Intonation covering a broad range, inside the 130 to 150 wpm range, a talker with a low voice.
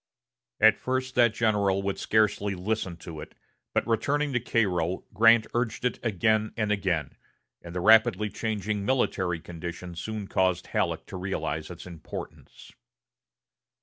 No: average, 3.8 semitones; average, 140 wpm; low, 105 Hz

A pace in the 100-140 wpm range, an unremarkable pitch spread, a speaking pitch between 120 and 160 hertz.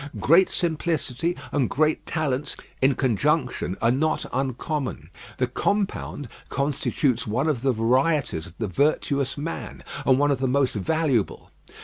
Yes: slow, 135 wpm; average, 3.7 semitones; medium, 140 Hz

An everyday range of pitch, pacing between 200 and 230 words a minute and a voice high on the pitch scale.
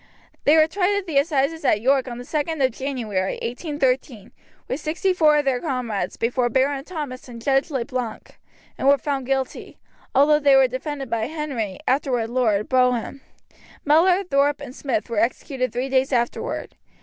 No: average, 3.1 semitones; average, 175 wpm; very high, 270 Hz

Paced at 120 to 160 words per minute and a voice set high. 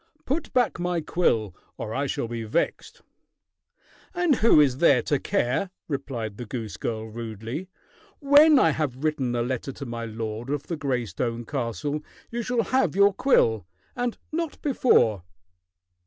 No: average, 155 wpm; low, 135 Hz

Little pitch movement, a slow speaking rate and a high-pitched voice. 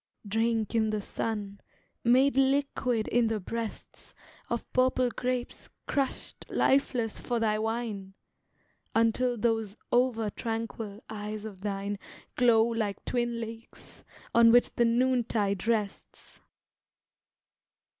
Yes: narrow, 2.3 semitones; slow, 110 wpm; high, 225 Hz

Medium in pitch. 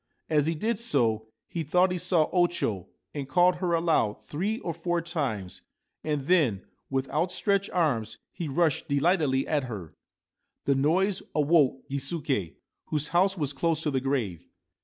Yes: medium, 155 Hz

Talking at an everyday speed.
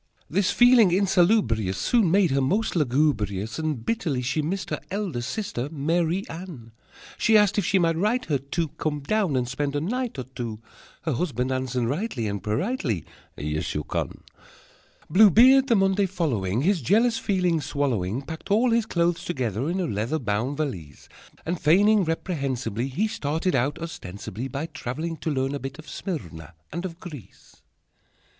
Yes: average, 170 wpm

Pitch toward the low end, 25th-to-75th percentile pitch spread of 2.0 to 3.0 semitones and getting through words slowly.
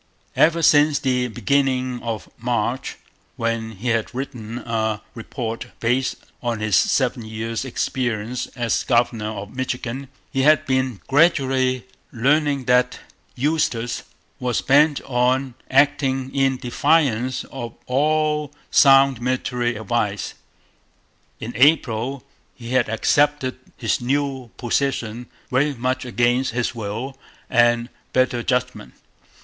Yes: low, 125 Hz; narrow, 2.6 semitones; slow, 115 wpm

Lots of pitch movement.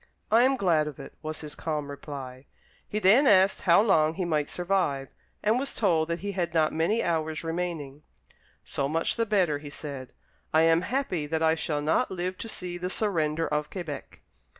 No: average, 3.9 semitones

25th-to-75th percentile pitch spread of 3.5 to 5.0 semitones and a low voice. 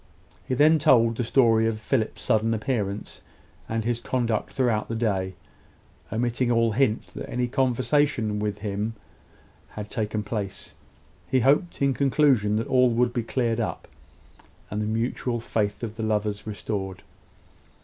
No: average, 2.8 semitones; low, 115 Hz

